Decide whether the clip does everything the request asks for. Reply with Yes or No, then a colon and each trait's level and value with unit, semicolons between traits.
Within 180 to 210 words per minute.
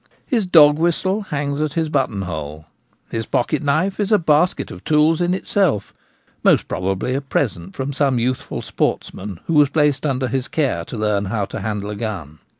Yes: average, 185 wpm